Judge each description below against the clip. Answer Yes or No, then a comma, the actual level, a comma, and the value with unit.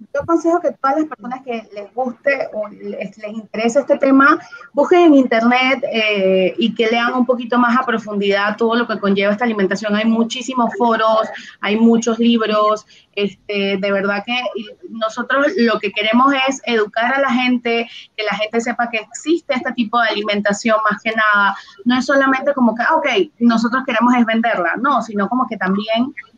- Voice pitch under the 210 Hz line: No, high, 230 Hz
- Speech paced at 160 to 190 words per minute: Yes, average, 185 wpm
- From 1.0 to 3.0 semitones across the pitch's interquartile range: No, average, 3.4 semitones